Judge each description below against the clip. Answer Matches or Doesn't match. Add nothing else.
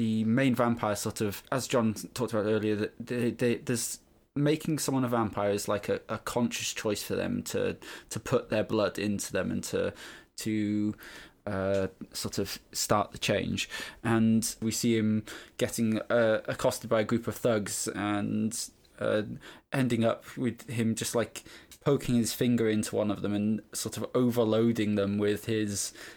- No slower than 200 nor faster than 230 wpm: Doesn't match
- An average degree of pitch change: Doesn't match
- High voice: Doesn't match